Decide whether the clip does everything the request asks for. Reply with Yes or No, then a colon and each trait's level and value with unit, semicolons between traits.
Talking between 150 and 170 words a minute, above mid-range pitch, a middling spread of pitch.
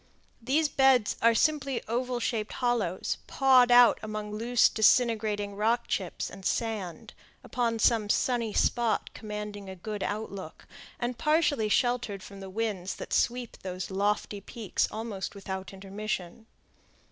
No: slow, 135 wpm; high, 220 Hz; average, 3.2 semitones